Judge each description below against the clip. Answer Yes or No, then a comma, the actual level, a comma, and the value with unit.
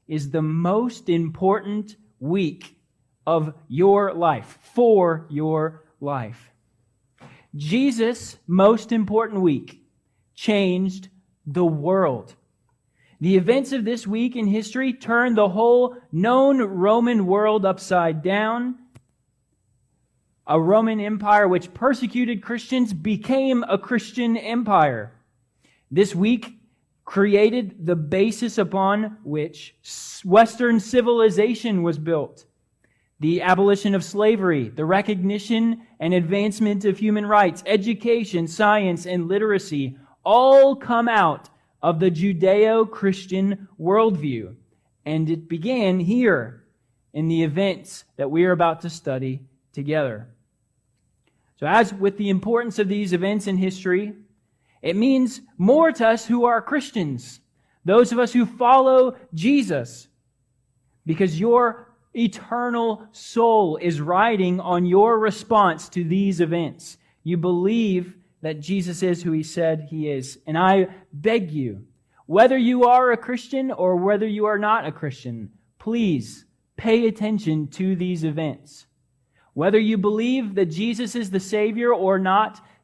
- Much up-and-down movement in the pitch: Yes, wide, 5.9 semitones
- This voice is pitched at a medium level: No, high, 195 Hz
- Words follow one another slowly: Yes, slow, 120 wpm